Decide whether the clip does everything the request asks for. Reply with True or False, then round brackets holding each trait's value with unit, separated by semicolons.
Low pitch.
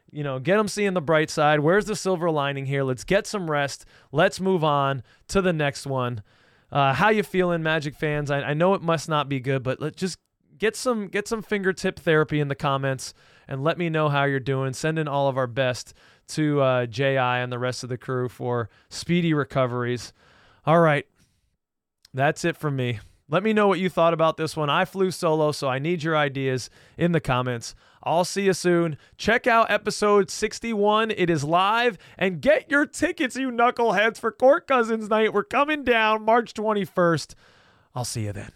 False (155 Hz)